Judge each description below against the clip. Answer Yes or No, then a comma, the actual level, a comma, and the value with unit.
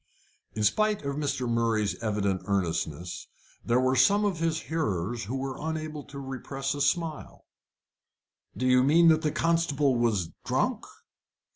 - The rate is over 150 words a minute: No, average, 145 wpm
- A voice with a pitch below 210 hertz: Yes, low, 135 Hz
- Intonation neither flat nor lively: No, wide, 5.7 semitones